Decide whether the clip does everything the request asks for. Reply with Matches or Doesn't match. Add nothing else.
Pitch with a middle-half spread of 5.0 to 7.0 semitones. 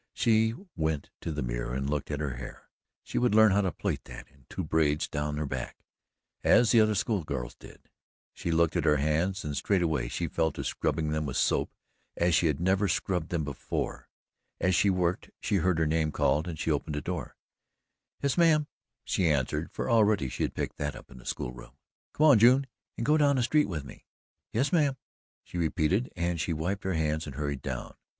Matches